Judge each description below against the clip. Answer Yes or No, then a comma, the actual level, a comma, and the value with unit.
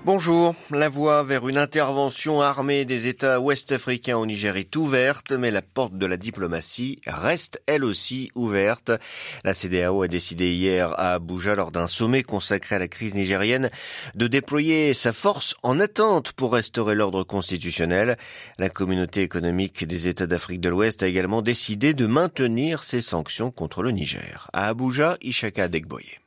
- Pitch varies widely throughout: Yes, wide, 6.5 semitones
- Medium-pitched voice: No, low, 115 Hz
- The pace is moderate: Yes, average, 160 wpm